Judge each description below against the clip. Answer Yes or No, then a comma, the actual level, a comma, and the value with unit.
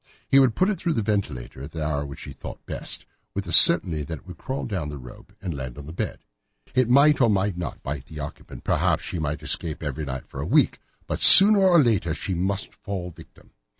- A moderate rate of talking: No, fast, 240 wpm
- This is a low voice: Yes, very low, 85 Hz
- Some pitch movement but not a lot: No, wide, 7.6 semitones